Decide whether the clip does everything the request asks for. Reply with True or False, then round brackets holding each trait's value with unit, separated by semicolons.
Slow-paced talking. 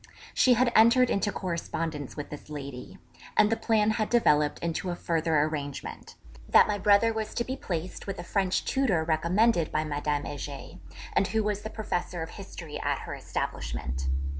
False (175 wpm)